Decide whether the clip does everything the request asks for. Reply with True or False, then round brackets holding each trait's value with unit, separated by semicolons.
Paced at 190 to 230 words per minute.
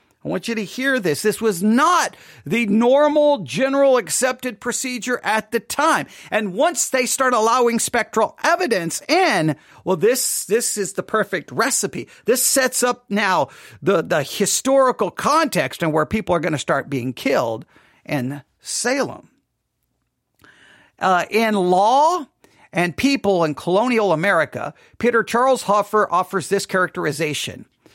False (140 wpm)